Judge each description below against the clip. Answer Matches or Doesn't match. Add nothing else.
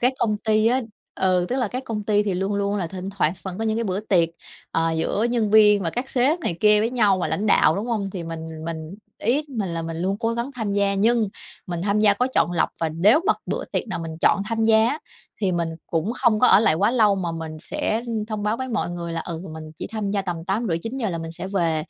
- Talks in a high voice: Matches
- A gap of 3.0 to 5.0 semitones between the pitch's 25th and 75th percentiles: Matches